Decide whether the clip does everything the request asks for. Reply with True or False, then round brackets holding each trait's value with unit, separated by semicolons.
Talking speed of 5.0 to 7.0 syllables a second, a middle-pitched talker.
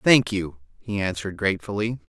False (5.9 syllables/s; 100 Hz)